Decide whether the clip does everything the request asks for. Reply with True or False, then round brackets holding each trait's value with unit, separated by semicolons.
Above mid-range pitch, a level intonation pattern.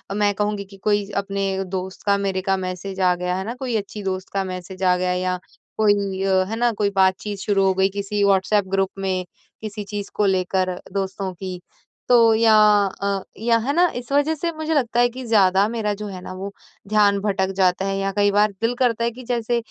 True (200 Hz; 2.2 semitones)